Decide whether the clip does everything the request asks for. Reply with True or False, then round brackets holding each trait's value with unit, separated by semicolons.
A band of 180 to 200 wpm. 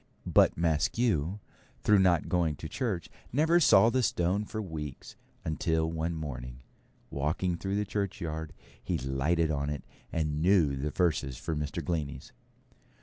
False (145 wpm)